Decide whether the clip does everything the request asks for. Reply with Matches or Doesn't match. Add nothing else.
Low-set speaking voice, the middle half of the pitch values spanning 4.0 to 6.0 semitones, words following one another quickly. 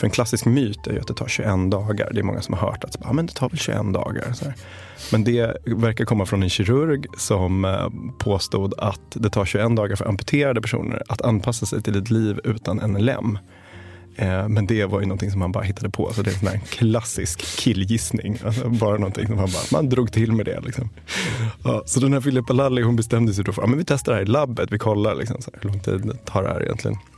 Doesn't match